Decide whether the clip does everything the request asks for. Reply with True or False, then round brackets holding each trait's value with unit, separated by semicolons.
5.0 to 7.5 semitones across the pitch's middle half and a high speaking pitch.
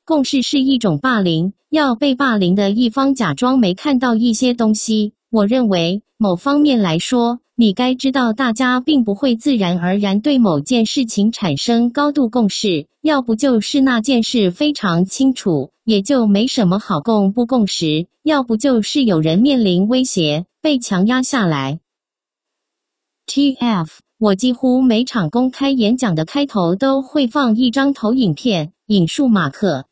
True (5.3 semitones; 235 Hz)